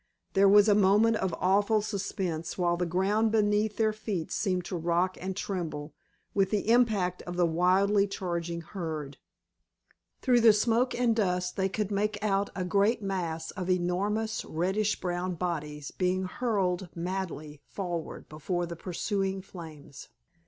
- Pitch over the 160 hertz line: Yes, high, 190 Hz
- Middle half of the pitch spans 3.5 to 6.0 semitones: No, average, 3.0 semitones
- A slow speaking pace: No, average, 150 wpm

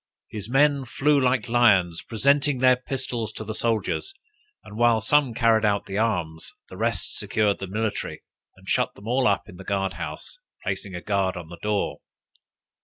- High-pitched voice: No, low, 110 Hz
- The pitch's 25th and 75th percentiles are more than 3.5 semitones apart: Yes, average, 4.3 semitones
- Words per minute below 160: No, average, 180 wpm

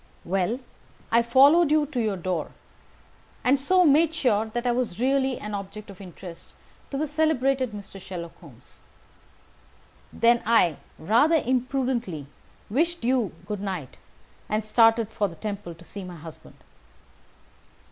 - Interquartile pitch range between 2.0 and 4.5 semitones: No, wide, 5.5 semitones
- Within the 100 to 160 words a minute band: Yes, average, 140 wpm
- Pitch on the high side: Yes, high, 230 Hz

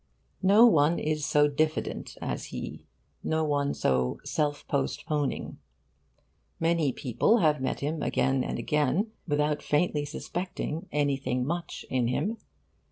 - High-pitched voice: No, medium, 150 Hz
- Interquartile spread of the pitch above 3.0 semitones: No, narrow, 2.5 semitones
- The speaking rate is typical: No, slow, 125 wpm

